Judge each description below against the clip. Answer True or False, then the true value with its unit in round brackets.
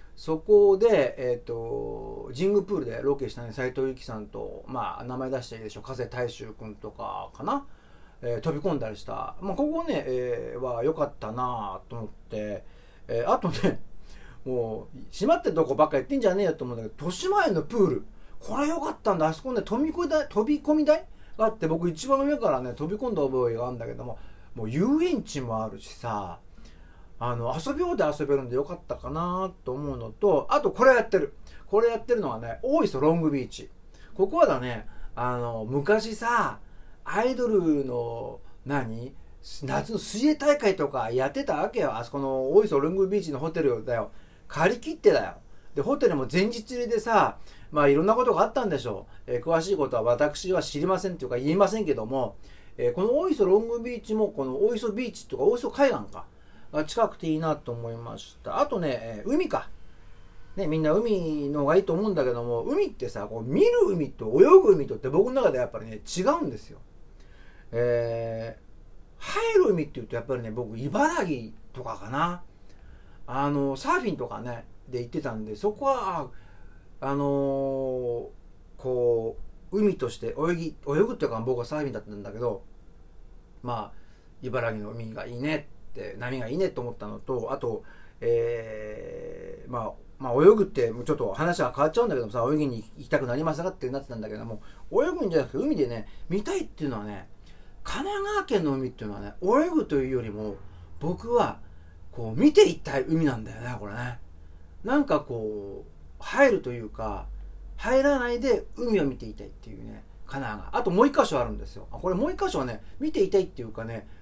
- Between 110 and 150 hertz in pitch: True (135 Hz)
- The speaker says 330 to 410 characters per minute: True (360 characters per minute)